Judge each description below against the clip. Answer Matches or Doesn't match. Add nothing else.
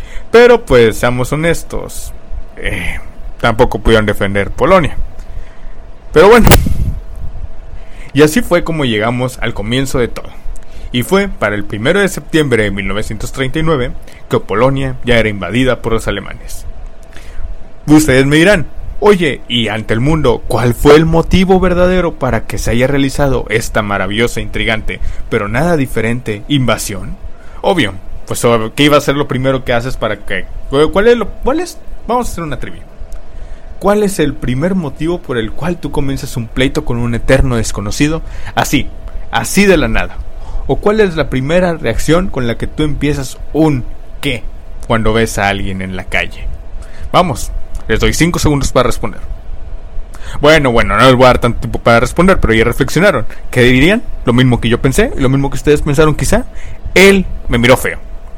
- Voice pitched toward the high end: Doesn't match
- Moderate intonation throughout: Doesn't match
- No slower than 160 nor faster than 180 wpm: Matches